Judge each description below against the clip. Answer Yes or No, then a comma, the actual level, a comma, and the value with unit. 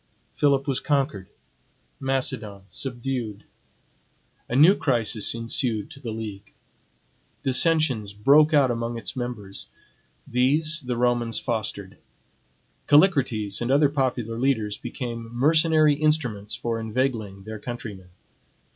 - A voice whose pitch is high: No, low, 120 Hz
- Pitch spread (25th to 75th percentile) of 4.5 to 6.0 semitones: No, average, 4.1 semitones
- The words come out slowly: Yes, slow, 110 wpm